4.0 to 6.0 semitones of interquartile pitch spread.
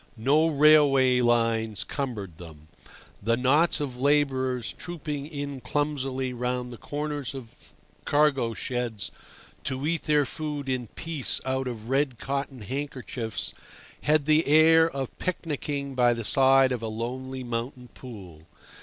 No: average, 3.4 semitones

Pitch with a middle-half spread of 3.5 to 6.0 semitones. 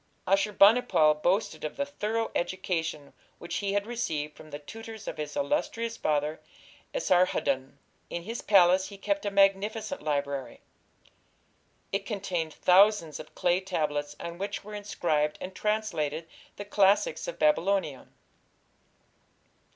Yes: average, 5.3 semitones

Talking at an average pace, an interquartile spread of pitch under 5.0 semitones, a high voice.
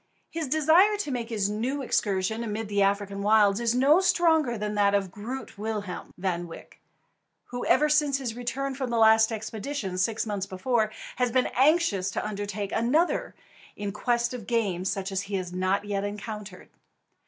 Yes: average, 175 wpm; average, 4.1 semitones; high, 220 Hz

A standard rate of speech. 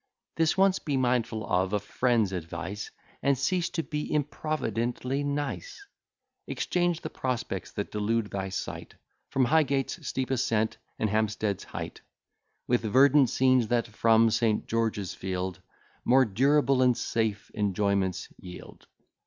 No: slow, 130 wpm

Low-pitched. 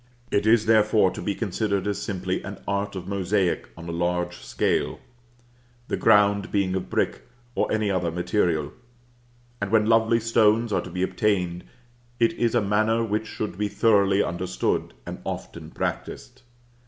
Yes: low, 100 Hz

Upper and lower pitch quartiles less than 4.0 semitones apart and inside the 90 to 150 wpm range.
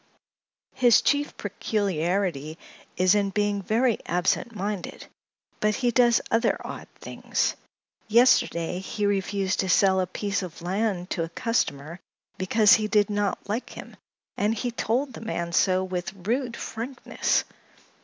Yes: average, 3.5 semitones; average, 140 wpm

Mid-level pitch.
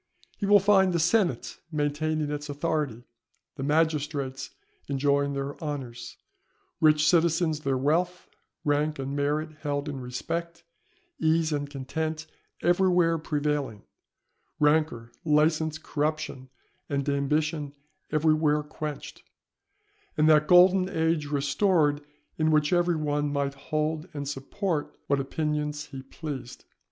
Yes: medium, 150 Hz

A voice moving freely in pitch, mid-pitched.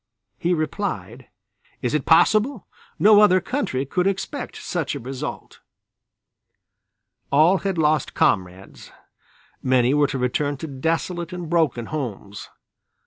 Yes: wide, 5.9 semitones; medium, 155 Hz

